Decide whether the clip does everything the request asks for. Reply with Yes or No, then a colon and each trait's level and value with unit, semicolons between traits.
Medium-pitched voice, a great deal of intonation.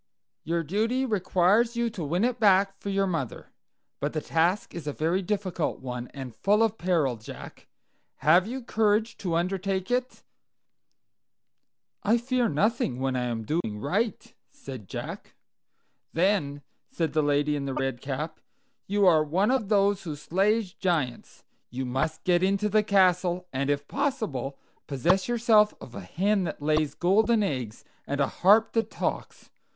Yes: medium, 180 Hz; wide, 6.4 semitones